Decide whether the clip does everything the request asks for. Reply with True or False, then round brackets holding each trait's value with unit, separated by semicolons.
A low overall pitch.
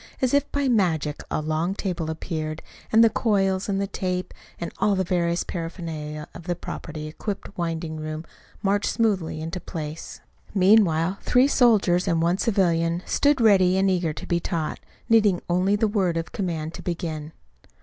False (180 Hz)